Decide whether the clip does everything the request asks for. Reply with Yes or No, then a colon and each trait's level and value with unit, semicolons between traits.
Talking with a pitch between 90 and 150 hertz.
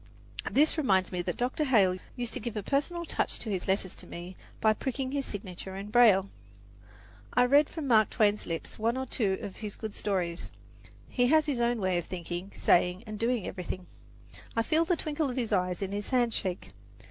No: high, 215 Hz